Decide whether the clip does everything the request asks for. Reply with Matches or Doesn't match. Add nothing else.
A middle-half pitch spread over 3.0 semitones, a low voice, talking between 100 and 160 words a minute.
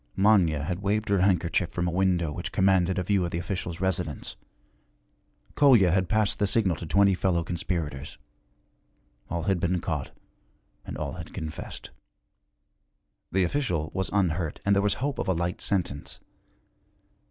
Doesn't match